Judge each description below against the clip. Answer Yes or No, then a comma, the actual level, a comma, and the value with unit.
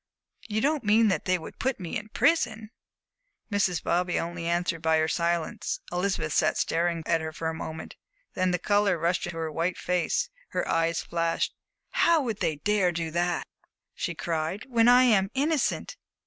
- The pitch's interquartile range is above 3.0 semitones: Yes, average, 4.3 semitones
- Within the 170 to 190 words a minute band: Yes, average, 175 wpm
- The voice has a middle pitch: Yes, medium, 175 Hz